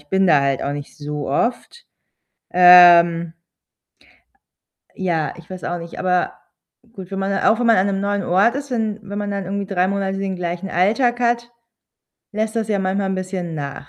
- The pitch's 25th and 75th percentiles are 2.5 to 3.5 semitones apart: Yes, average, 2.9 semitones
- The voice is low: No, high, 190 Hz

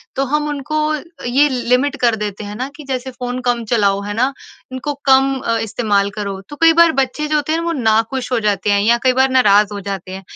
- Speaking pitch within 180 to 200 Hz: No, very high, 250 Hz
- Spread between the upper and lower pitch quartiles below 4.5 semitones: No, average, 4.8 semitones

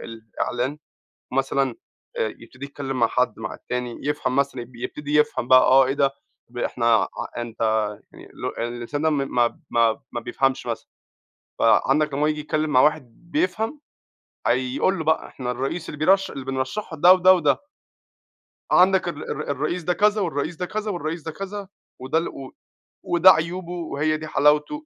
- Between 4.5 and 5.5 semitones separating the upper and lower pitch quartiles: Yes, average, 5.0 semitones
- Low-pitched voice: No, medium, 145 Hz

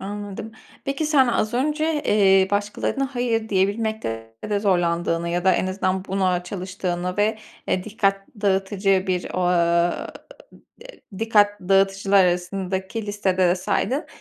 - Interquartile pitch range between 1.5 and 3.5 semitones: Yes, narrow, 2.6 semitones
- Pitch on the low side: No, high, 195 Hz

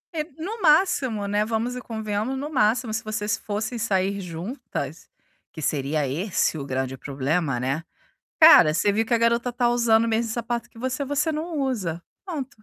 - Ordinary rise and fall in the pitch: No, wide, 6.1 semitones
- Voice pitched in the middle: No, high, 220 Hz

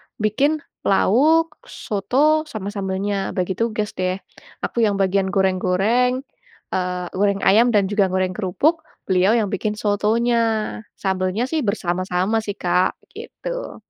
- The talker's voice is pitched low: No, high, 205 Hz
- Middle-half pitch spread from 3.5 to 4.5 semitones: Yes, average, 3.8 semitones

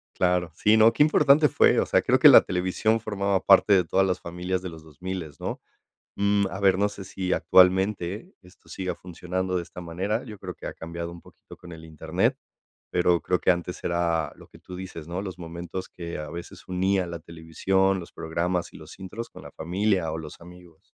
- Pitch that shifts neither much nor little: No, narrow, 2.3 semitones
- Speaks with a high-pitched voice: No, very low, 90 Hz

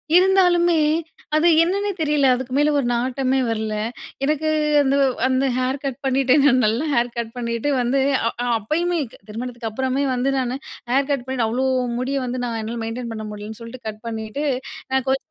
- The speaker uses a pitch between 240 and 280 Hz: Yes, very high, 255 Hz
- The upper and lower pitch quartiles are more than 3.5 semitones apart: No, average, 3.2 semitones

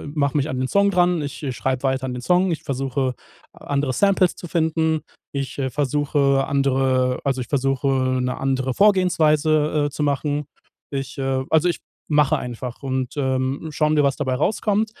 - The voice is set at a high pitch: No, medium, 140 Hz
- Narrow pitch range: No, average, 3.0 semitones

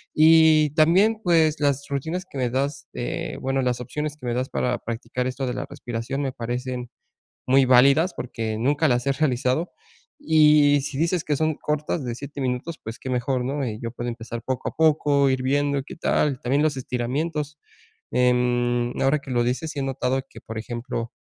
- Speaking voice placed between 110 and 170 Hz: Yes, low, 135 Hz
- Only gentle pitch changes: No, average, 3.4 semitones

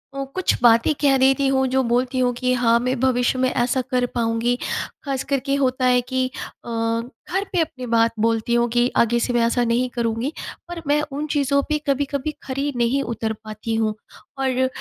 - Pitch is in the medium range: No, very high, 255 Hz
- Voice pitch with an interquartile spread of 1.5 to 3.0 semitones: Yes, narrow, 2.4 semitones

